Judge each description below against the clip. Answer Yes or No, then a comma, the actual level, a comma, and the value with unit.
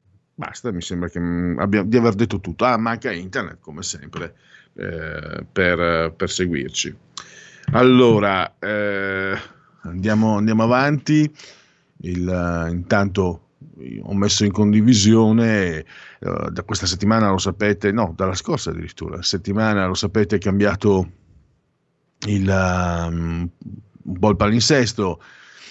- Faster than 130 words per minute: No, average, 125 wpm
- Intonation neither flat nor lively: Yes, average, 3.4 semitones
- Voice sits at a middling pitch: No, low, 100 Hz